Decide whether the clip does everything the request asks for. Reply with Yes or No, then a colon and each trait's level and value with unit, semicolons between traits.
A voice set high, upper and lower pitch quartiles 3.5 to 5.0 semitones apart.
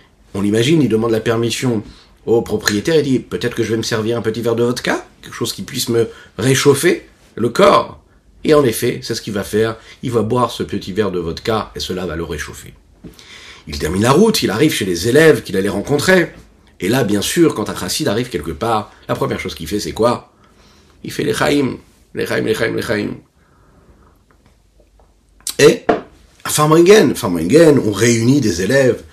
No: low, 115 Hz; average, 3.8 semitones